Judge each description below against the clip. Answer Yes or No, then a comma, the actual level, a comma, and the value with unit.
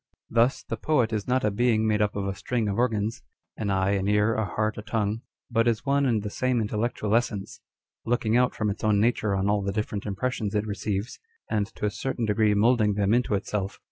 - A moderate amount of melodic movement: No, narrow, 2.3 semitones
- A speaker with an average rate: No, fast, 235 wpm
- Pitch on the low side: Yes, low, 110 Hz